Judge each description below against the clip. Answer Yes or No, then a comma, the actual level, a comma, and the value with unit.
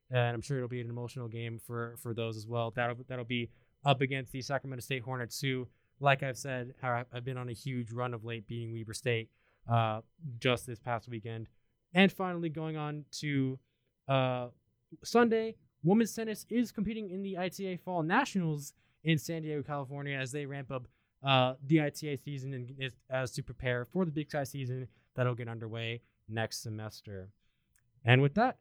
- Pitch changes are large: No, average, 3.7 semitones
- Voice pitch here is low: Yes, low, 130 Hz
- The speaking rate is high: No, average, 185 wpm